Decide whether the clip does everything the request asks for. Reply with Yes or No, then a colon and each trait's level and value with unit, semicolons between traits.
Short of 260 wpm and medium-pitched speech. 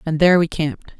Yes: fast, 240 wpm; medium, 160 Hz